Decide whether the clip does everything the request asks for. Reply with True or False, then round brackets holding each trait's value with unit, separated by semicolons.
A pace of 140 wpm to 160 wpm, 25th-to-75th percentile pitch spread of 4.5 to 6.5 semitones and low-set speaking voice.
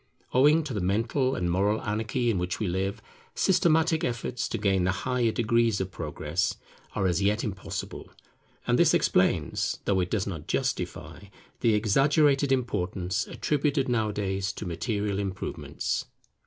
True (145 wpm; 4.8 semitones; 105 Hz)